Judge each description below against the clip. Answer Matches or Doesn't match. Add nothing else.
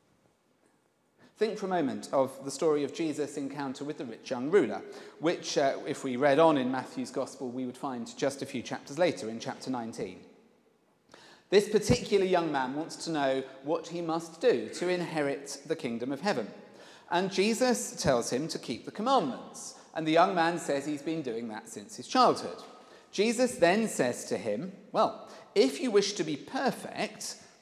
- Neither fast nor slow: Matches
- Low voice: Doesn't match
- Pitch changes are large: Matches